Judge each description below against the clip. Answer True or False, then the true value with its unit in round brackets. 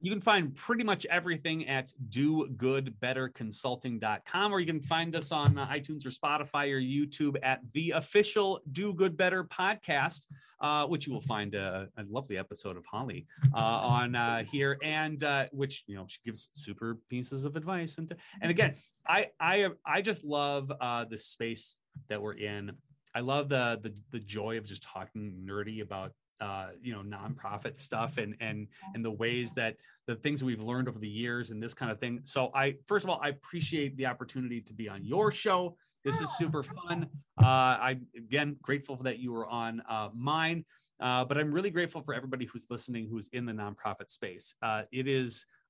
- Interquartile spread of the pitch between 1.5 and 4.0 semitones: False (4.7 semitones)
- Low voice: True (130 Hz)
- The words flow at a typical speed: True (195 wpm)